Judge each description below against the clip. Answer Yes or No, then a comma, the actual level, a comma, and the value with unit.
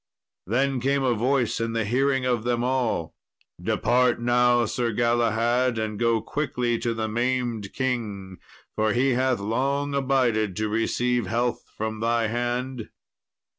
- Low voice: Yes, low, 120 Hz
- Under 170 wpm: Yes, average, 140 wpm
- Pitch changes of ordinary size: No, narrow, 2.2 semitones